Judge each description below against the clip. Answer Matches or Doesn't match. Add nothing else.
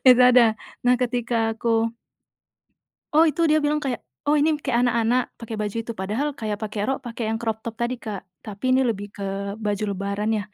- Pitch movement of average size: Matches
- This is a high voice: Matches